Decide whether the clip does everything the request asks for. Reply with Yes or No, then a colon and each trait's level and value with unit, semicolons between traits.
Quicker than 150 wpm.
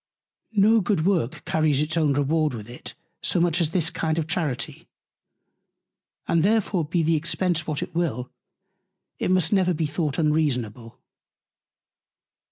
No: average, 145 wpm